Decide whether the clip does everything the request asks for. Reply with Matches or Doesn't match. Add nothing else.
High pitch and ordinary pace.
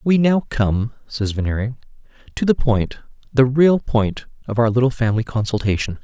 Doesn't match